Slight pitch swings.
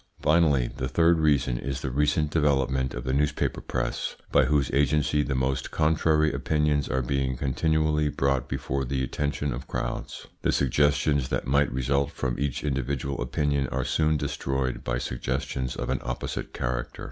Yes: narrow, 2.3 semitones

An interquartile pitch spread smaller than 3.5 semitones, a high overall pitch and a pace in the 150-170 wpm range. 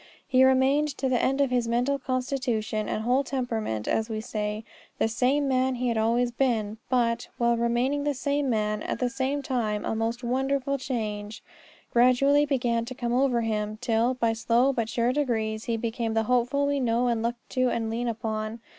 No: average, 2.7 semitones; high, 240 Hz; average, 190 wpm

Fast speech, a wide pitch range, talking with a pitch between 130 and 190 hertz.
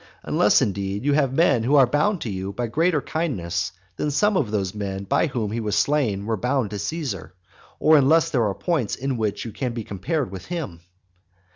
No: fast, 210 wpm; wide, 6.8 semitones; low, 120 Hz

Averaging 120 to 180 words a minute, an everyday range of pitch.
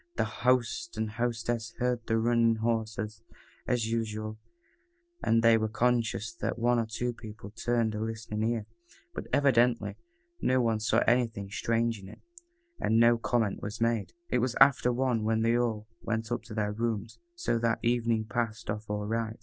No: average, 175 wpm; narrow, 1.5 semitones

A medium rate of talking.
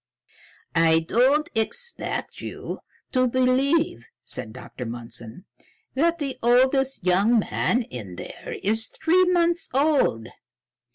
No: slow, 110 wpm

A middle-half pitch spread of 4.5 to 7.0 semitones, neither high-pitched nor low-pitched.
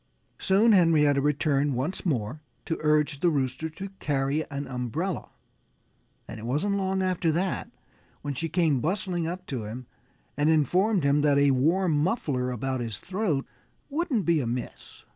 Yes: average, 5.1 semitones; medium, 150 Hz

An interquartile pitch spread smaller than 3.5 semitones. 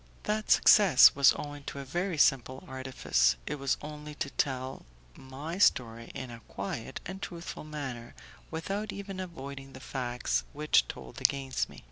No: average, 3.9 semitones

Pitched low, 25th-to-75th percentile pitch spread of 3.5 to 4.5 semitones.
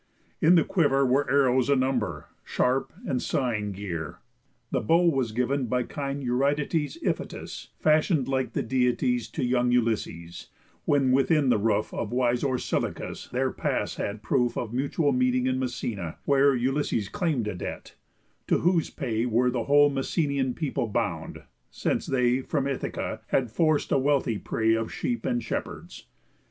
No: low, 130 Hz; average, 3.0 semitones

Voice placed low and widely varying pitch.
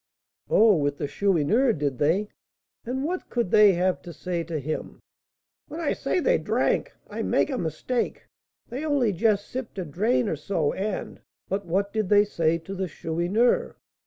No: high, 200 Hz; wide, 5.8 semitones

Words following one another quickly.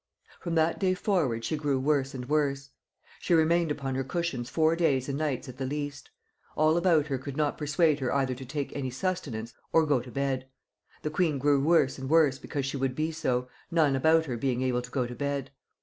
Yes: fast, 215 wpm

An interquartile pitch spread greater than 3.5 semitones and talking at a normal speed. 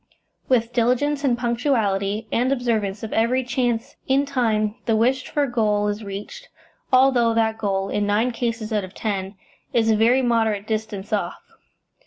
No: average, 3.0 semitones; average, 160 wpm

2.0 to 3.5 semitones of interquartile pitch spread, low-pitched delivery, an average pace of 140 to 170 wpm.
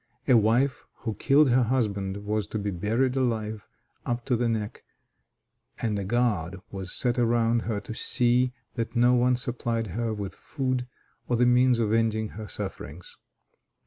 Yes: average, 2.7 semitones; low, 115 Hz; average, 165 wpm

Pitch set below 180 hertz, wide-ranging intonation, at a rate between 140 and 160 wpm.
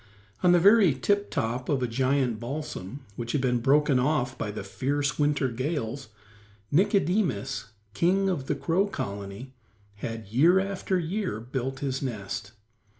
Yes: low, 135 Hz; wide, 6.0 semitones; average, 150 wpm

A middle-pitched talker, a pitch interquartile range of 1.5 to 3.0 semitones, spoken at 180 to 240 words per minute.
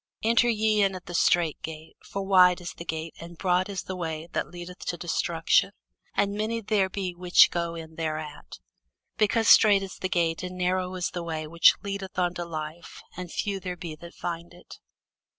Yes: medium, 180 Hz; narrow, 2.4 semitones; average, 195 wpm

